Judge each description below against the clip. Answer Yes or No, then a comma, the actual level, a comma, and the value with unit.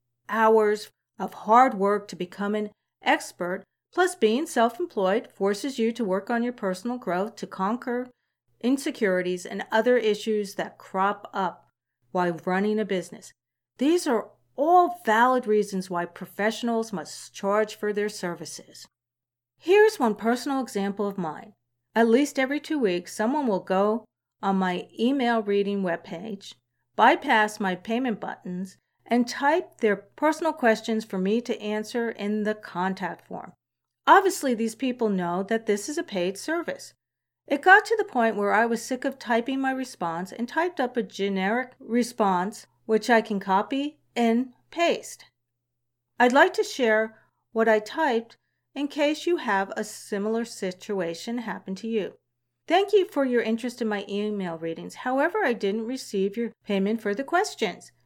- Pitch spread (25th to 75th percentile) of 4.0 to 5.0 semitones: Yes, average, 4.3 semitones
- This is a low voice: No, high, 220 Hz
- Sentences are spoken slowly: No, average, 155 wpm